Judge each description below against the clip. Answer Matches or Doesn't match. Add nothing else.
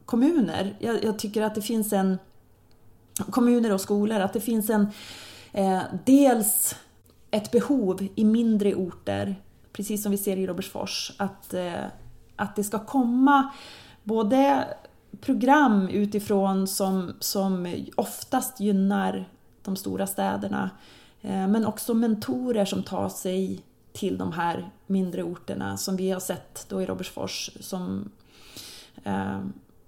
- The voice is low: Doesn't match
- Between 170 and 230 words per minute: Doesn't match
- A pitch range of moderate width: Matches